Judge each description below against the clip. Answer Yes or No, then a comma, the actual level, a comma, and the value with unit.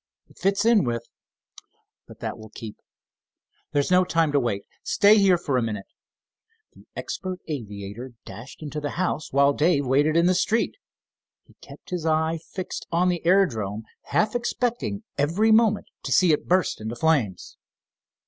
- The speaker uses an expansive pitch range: Yes, wide, 6.9 semitones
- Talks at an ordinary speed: Yes, average, 160 wpm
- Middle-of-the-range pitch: Yes, medium, 160 Hz